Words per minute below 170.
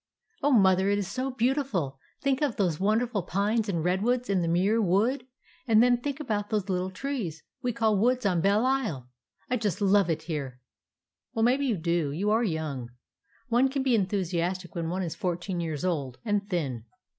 No: average, 190 wpm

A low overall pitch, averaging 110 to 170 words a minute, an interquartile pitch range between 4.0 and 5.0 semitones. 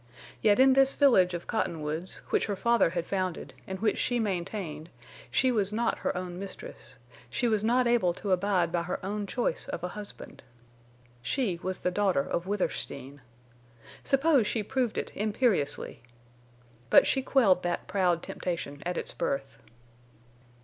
No: high, 190 Hz; average, 155 wpm; average, 4.7 semitones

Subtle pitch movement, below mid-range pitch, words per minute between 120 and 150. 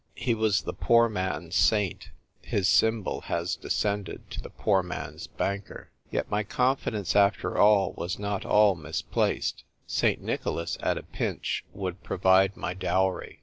Yes: narrow, 2.3 semitones; low, 100 Hz; average, 145 wpm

